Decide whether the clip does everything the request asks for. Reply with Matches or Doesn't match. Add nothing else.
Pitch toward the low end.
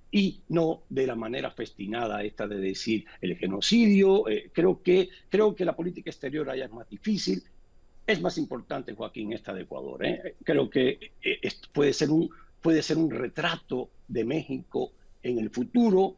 Doesn't match